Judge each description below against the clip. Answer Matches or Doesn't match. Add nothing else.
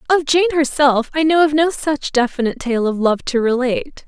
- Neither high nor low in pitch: Doesn't match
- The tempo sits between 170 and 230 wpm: Matches